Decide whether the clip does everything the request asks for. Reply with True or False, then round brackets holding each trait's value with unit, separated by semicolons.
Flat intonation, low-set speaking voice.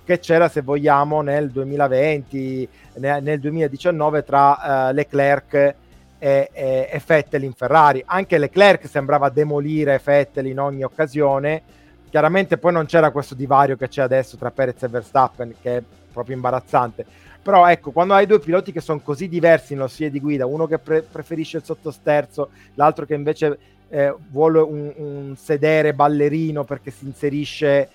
False (2.3 semitones; 145 Hz)